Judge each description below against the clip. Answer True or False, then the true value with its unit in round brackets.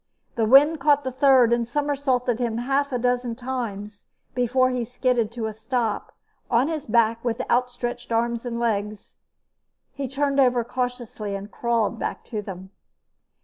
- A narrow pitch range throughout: True (2.3 semitones)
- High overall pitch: True (245 Hz)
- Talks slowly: False (155 wpm)